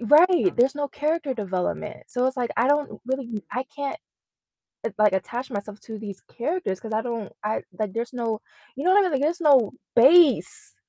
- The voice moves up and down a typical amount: Yes, average, 5.0 semitones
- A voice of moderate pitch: No, very high, 250 Hz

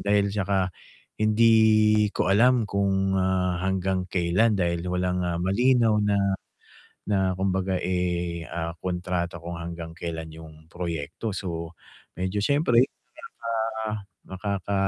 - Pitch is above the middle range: No, very low, 95 Hz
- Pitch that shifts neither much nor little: Yes, average, 3.1 semitones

